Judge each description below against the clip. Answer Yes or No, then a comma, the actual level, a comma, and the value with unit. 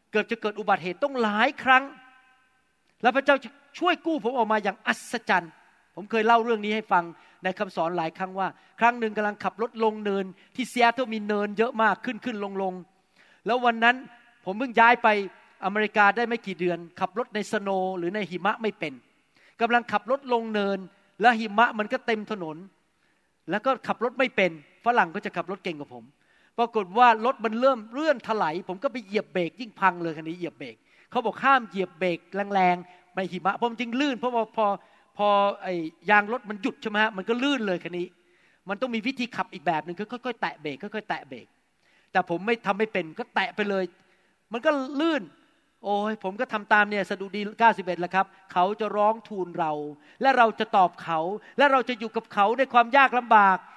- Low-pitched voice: No, high, 210 Hz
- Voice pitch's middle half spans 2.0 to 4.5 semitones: Yes, average, 4.1 semitones